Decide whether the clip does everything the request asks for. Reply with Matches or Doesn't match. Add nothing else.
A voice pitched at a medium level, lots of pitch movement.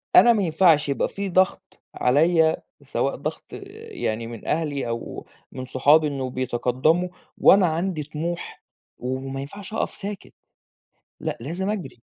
Matches